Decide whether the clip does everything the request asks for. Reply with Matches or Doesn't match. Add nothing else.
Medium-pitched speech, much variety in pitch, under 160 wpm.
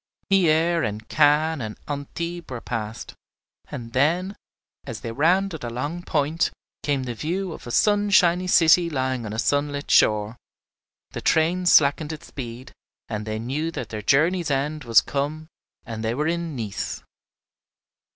Matches